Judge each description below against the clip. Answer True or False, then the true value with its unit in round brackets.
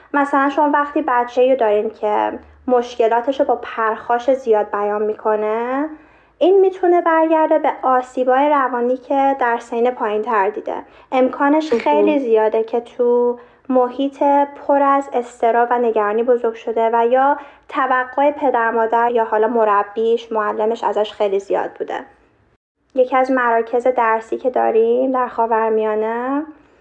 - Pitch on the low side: False (245 Hz)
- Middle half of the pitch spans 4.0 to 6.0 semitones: False (3.5 semitones)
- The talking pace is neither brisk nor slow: True (135 wpm)